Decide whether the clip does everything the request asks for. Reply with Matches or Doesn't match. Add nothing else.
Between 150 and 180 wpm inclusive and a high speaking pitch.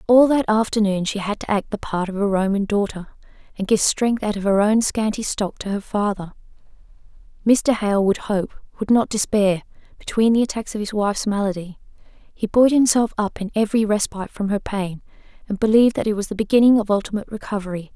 Doesn't match